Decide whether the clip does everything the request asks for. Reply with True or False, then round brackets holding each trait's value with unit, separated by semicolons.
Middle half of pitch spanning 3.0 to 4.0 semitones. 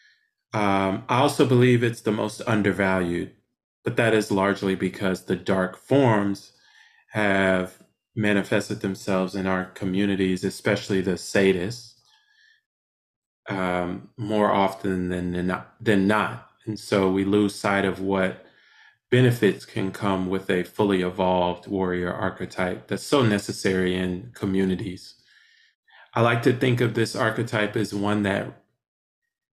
True (3.5 semitones)